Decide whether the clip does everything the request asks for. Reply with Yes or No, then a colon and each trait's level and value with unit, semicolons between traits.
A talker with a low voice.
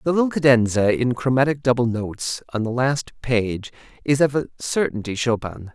Yes: low, 125 Hz